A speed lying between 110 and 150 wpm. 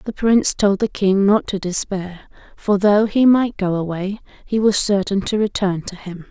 No: average, 200 wpm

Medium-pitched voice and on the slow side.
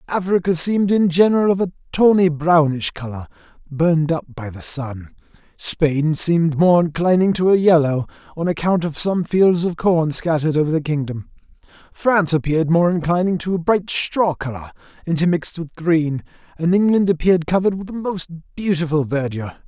No: medium, 165 Hz; average, 160 wpm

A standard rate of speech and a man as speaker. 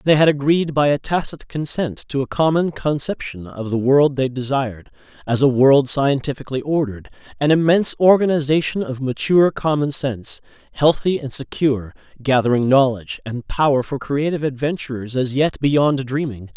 Yes: average, 150 wpm; male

